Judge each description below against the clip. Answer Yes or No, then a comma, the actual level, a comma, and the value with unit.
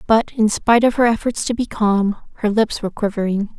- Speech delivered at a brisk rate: Yes, fast, 220 wpm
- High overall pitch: Yes, high, 215 Hz